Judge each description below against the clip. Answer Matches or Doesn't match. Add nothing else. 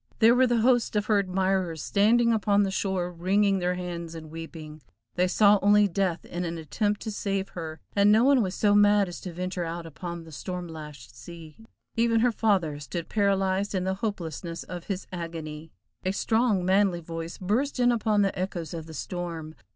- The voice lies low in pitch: Doesn't match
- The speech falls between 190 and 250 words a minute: Matches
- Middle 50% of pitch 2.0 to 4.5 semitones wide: Matches